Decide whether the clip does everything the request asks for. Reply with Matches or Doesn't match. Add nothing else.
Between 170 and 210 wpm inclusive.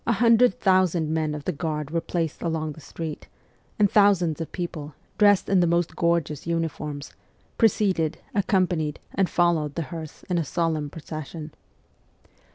Doesn't match